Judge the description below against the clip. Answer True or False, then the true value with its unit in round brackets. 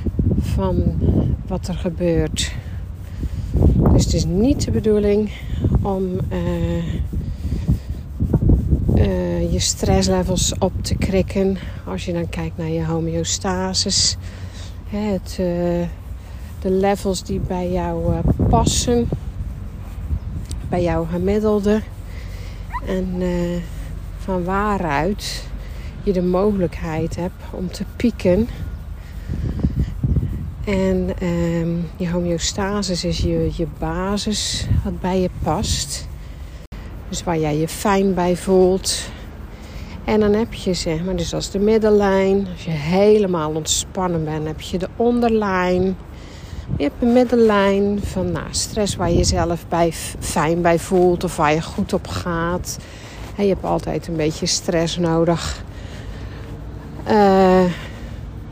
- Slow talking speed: True (120 wpm)